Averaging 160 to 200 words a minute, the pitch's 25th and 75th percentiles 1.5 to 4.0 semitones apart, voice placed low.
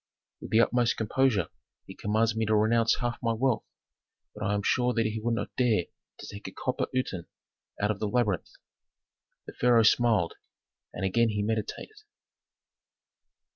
Yes: average, 165 wpm; narrow, 2.5 semitones; low, 115 Hz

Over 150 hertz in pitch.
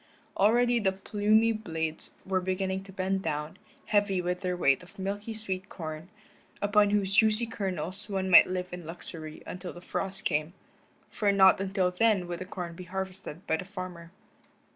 Yes: high, 190 Hz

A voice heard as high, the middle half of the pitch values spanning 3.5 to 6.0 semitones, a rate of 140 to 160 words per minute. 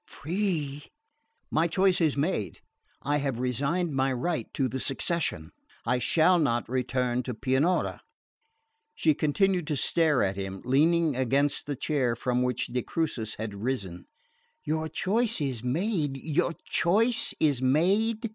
No: medium, 145 Hz; average, 5.2 semitones; average, 145 wpm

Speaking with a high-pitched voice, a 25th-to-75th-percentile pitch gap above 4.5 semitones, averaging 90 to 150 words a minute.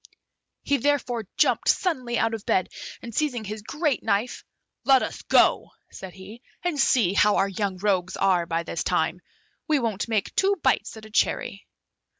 No: high, 220 Hz; average, 5.1 semitones; average, 170 wpm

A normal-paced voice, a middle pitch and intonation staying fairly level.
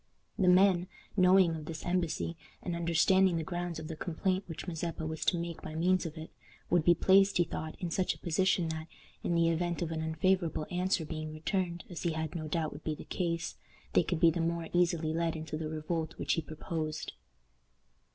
No: fast, 210 wpm; medium, 170 Hz; narrow, 2.0 semitones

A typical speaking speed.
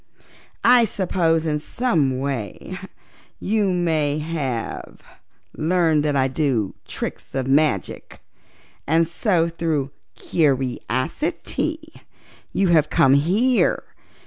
No: slow, 95 wpm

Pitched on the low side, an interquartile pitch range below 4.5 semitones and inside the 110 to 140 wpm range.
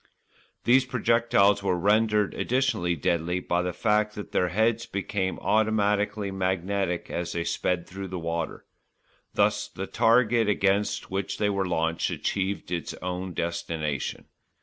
Yes: low, 100 Hz; average, 3.2 semitones; slow, 135 wpm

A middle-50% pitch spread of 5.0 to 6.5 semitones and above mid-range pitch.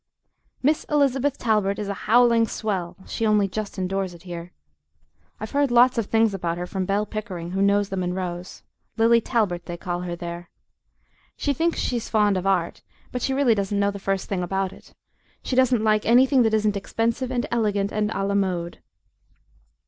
No: average, 3.8 semitones; high, 205 Hz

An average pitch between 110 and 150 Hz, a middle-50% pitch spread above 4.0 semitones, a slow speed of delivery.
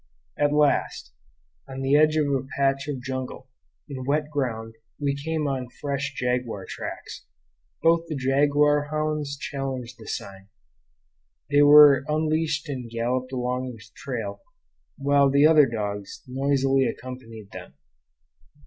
No: low, 135 Hz; average, 2.7 semitones; slow, 130 wpm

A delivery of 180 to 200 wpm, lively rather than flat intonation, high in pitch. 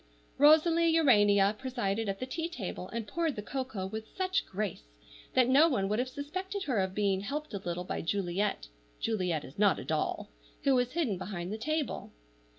Yes: average, 185 wpm; wide, 7.1 semitones; high, 220 Hz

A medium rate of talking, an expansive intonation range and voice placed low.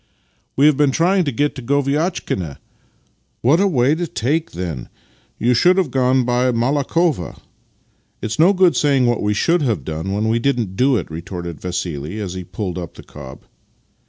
Yes: average, 190 wpm; wide, 8.0 semitones; low, 125 Hz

